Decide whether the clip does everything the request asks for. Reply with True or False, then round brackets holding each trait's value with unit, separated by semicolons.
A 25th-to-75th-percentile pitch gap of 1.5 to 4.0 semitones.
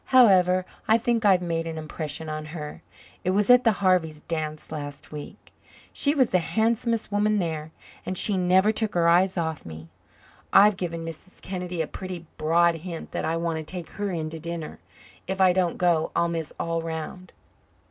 True (2.9 semitones)